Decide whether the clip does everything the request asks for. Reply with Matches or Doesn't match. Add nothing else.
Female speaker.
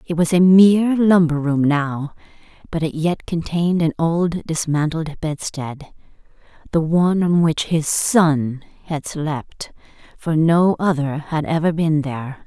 Matches